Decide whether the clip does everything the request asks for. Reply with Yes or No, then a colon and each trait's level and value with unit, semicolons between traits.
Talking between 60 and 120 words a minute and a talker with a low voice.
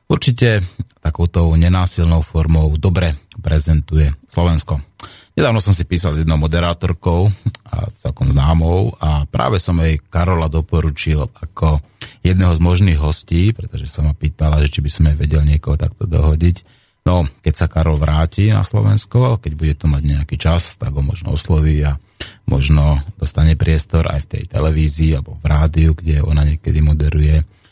No: average, 155 wpm; very low, 80 Hz